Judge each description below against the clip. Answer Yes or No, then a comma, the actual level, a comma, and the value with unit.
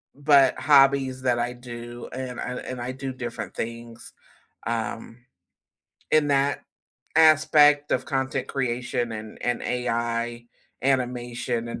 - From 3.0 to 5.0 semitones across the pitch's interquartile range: No, narrow, 2.4 semitones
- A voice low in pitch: Yes, low, 125 Hz